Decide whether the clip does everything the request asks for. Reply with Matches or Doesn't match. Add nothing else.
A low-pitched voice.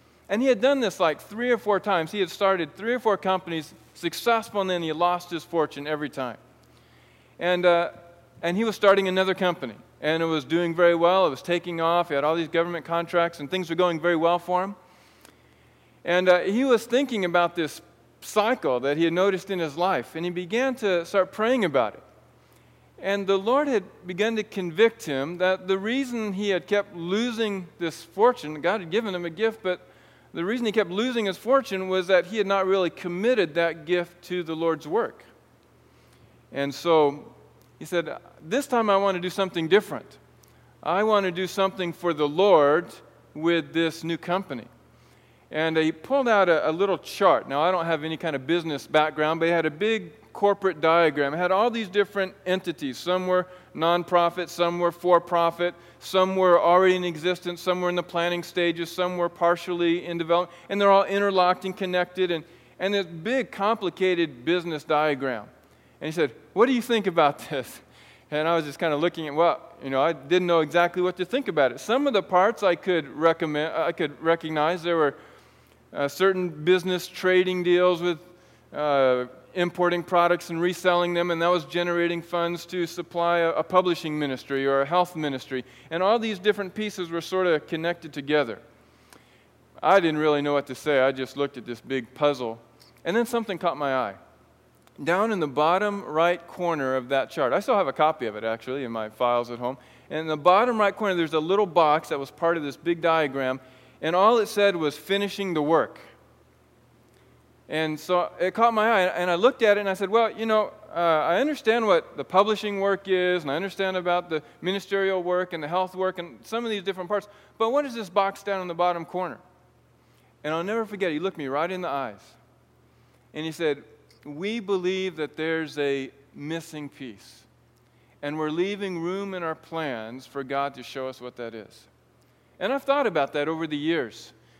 Doesn't match